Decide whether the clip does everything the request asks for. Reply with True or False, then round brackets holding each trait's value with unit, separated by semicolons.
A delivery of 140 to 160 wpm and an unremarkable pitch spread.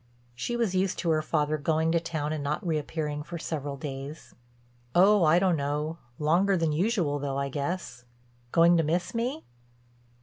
False (170 wpm; 3.1 semitones)